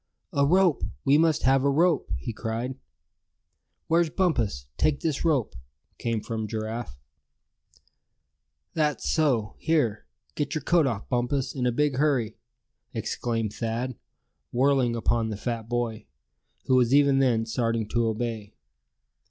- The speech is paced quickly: No, slow, 135 wpm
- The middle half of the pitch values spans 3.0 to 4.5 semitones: Yes, average, 4.2 semitones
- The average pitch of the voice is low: Yes, low, 125 Hz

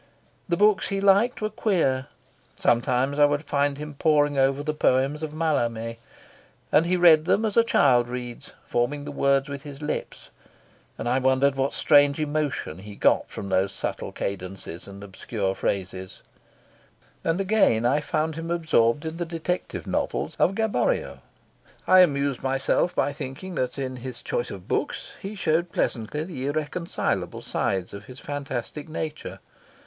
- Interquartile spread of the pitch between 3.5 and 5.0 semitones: Yes, average, 4.5 semitones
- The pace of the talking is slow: No, average, 160 wpm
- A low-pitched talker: No, medium, 145 Hz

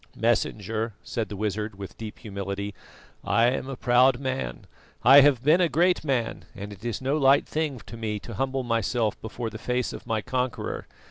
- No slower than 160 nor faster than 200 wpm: Yes, average, 190 wpm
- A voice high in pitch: No, low, 120 Hz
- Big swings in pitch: No, average, 3.6 semitones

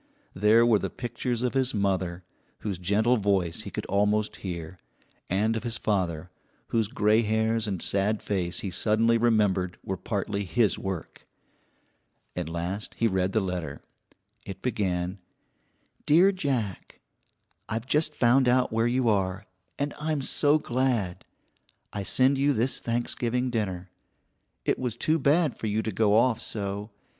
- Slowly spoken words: No, average, 150 wpm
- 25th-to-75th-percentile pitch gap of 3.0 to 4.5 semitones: Yes, average, 4.0 semitones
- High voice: No, low, 110 Hz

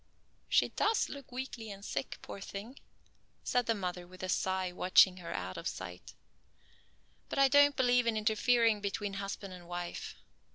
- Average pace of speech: Yes, average, 165 wpm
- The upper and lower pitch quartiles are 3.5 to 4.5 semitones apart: No, average, 5.1 semitones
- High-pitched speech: Yes, high, 200 Hz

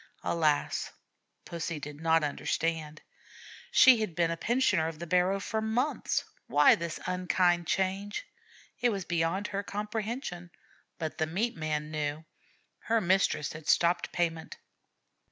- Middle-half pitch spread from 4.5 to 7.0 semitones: No, average, 4.0 semitones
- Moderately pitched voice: Yes, medium, 175 Hz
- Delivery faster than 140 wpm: No, slow, 135 wpm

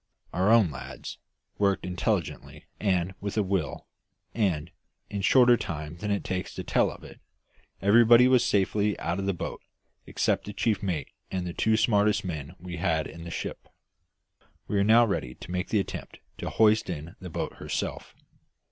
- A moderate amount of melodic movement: Yes, average, 3.6 semitones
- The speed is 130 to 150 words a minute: No, average, 180 wpm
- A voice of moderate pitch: No, very low, 95 Hz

